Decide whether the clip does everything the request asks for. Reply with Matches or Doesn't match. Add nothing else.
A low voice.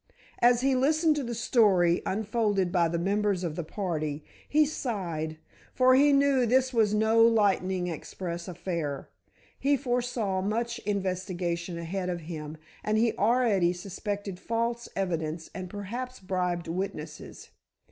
Doesn't match